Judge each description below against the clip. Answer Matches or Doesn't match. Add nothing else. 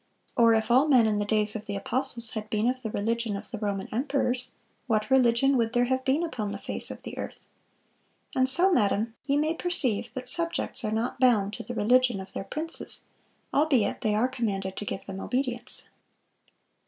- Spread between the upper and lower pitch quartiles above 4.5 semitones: Doesn't match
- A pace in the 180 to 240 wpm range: Matches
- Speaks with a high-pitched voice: Matches